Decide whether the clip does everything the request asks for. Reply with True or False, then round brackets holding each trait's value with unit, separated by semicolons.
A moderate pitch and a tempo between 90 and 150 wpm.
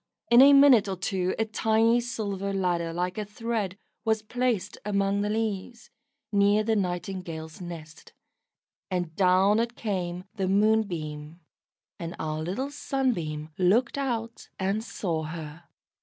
False (195 Hz; 135 wpm)